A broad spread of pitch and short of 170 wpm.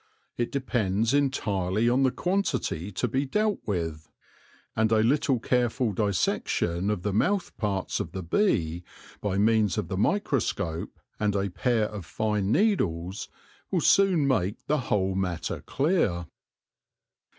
Yes: wide, 5.8 semitones; average, 140 wpm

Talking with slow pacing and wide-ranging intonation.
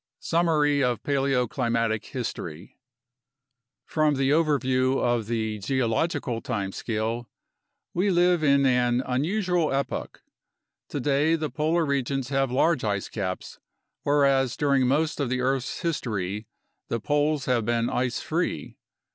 No: slow, 120 wpm; average, 3.8 semitones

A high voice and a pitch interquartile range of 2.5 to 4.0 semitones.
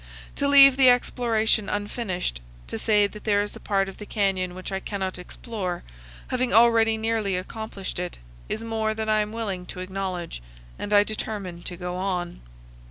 Yes: high, 205 Hz; average, 3.2 semitones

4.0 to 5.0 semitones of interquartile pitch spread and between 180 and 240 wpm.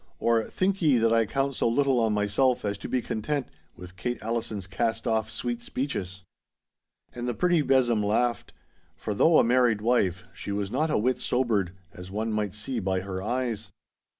No: average, 3.5 semitones; average, 185 wpm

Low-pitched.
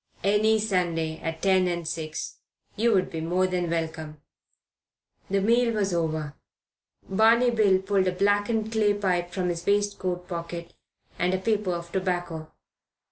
No: medium, 185 Hz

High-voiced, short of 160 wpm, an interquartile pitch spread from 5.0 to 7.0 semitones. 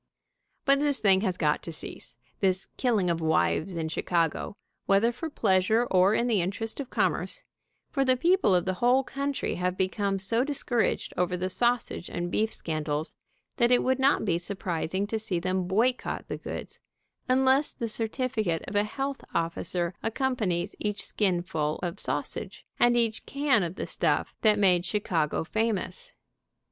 No: high, 205 Hz; average, 165 wpm; wide, 5.5 semitones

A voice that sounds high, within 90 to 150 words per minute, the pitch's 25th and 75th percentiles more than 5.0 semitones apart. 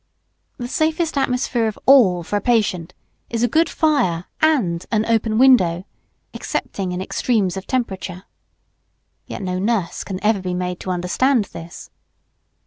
Yes: high, 210 Hz; average, 145 wpm; wide, 5.4 semitones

